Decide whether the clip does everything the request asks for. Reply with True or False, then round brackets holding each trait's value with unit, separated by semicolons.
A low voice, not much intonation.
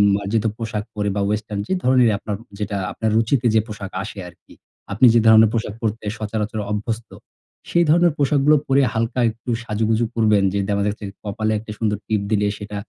True (110 Hz; 1.8 semitones)